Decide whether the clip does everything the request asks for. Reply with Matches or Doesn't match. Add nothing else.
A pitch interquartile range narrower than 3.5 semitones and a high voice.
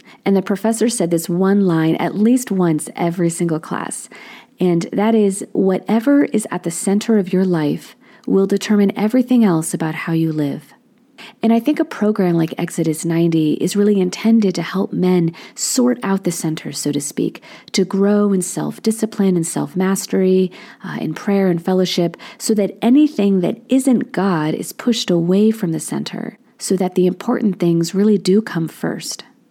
Doesn't match